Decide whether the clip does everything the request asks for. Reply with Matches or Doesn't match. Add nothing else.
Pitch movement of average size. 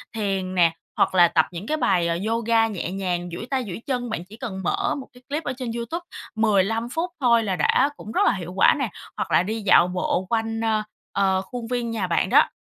Matches